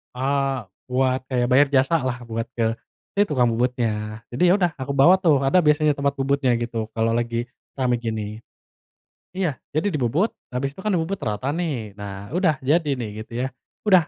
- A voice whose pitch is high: No, low, 130 Hz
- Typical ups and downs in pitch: Yes, average, 4.4 semitones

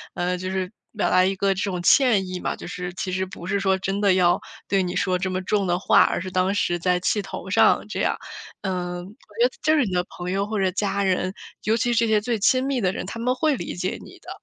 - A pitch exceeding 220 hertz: No, high, 190 Hz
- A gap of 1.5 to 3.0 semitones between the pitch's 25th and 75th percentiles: Yes, narrow, 2.5 semitones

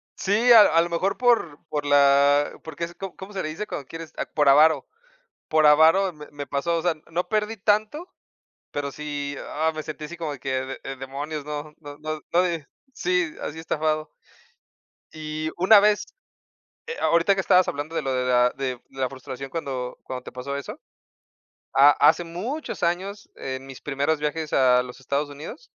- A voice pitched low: No, medium, 155 Hz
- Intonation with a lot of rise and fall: No, average, 3.6 semitones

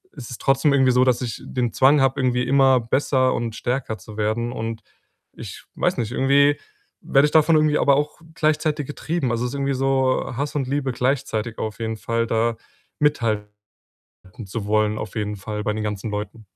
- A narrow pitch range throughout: No, average, 3.8 semitones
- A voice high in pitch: No, low, 125 Hz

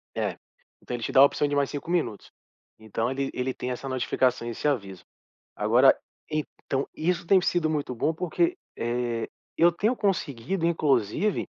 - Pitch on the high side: No, low, 135 Hz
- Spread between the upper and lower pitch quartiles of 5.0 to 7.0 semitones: Yes, wide, 5.5 semitones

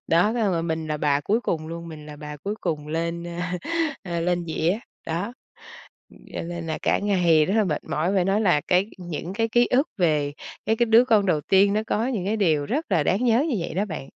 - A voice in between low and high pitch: Yes, medium, 175 Hz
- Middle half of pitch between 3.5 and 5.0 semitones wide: Yes, average, 4.6 semitones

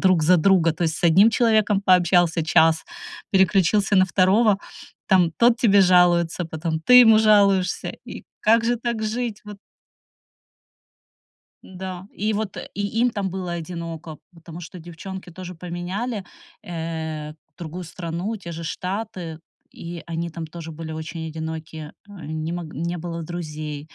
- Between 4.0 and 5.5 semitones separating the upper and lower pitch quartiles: No, average, 3.4 semitones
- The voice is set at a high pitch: No, medium, 175 Hz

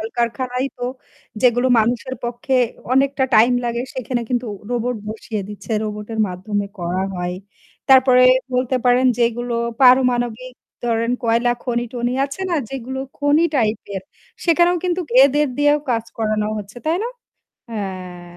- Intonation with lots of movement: No, average, 2.9 semitones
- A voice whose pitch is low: No, high, 240 Hz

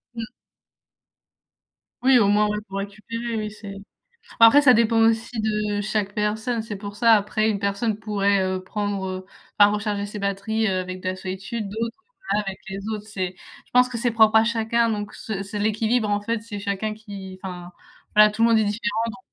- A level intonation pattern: Yes, narrow, 2.0 semitones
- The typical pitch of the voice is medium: No, high, 210 Hz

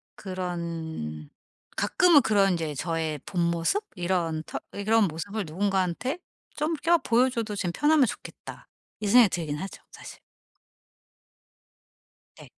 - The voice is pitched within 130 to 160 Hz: No, high, 190 Hz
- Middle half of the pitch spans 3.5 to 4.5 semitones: No, wide, 5.5 semitones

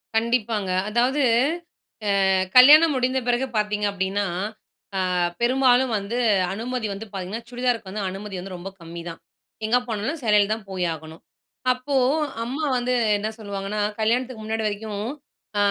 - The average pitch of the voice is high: Yes, high, 220 Hz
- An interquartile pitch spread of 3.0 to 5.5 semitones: Yes, average, 3.7 semitones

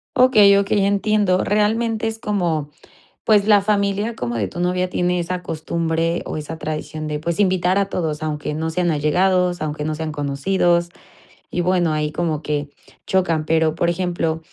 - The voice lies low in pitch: No, medium, 175 Hz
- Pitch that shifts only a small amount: No, average, 3.9 semitones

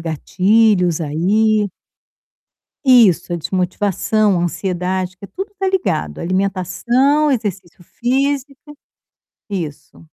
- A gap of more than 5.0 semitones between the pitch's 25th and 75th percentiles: Yes, wide, 5.6 semitones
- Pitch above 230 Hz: No, high, 195 Hz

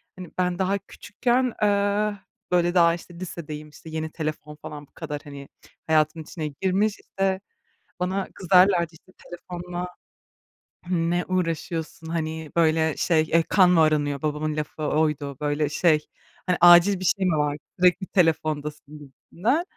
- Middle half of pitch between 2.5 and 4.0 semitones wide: Yes, average, 3.1 semitones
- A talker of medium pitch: Yes, medium, 165 Hz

